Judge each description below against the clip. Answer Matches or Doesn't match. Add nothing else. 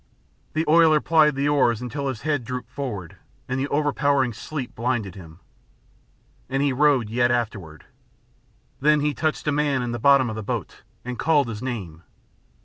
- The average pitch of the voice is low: Matches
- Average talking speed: Matches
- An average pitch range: Matches